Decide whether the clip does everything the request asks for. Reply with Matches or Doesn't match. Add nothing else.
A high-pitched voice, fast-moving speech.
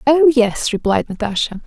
Doesn't match